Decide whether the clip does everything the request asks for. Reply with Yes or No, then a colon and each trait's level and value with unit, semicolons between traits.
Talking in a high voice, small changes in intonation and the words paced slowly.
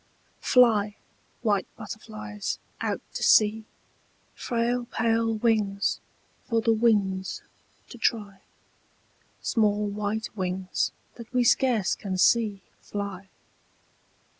Yes: high, 215 Hz; narrow, 2.3 semitones; slow, 95 wpm